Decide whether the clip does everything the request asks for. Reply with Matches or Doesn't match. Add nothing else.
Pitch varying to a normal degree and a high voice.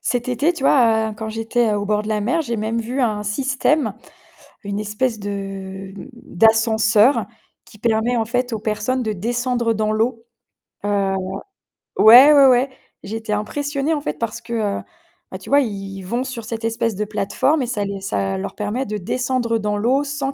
Matches